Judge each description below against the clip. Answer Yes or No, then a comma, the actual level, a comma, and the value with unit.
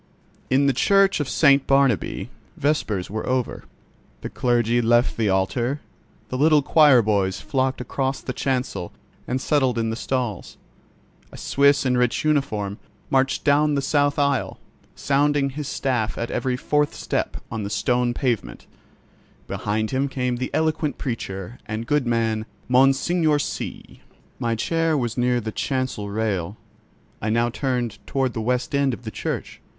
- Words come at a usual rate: Yes, average, 155 wpm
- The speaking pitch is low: Yes, low, 125 Hz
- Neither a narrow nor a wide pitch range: Yes, average, 3.6 semitones